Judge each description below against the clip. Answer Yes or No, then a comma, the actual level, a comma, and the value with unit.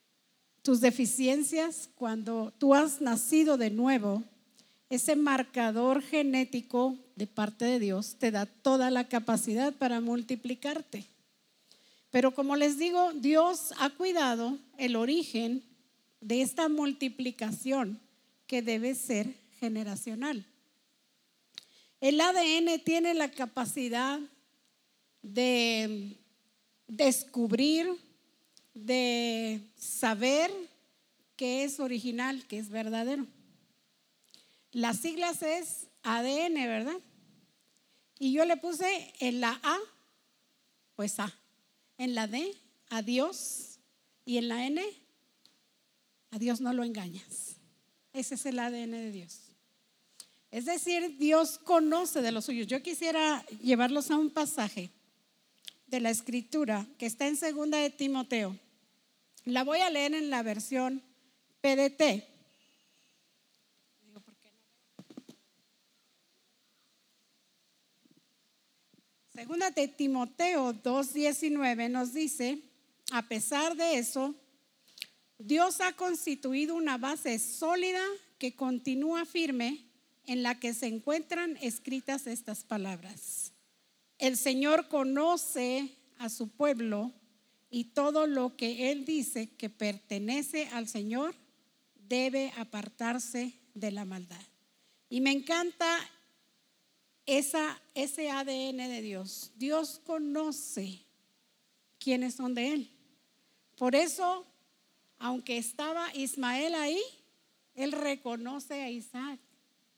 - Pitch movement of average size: Yes, average, 3.8 semitones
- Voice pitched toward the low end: No, very high, 255 Hz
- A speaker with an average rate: No, slow, 105 wpm